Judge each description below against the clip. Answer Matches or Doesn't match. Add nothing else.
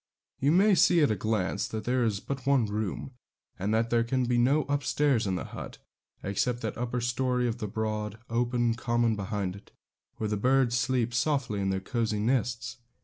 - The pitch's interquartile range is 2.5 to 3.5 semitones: Matches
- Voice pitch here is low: Matches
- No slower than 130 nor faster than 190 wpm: Doesn't match